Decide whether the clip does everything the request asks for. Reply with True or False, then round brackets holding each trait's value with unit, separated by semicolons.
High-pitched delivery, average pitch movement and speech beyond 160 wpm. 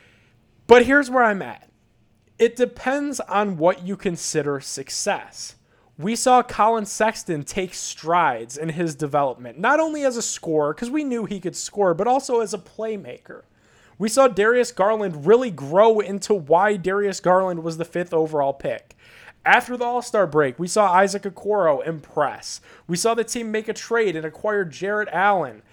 False (200 Hz; 5.8 semitones; 170 wpm)